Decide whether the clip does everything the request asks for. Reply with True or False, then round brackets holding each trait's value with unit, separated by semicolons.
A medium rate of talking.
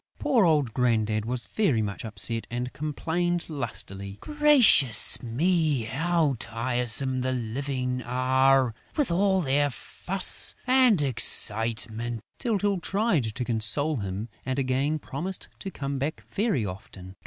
False (125 wpm)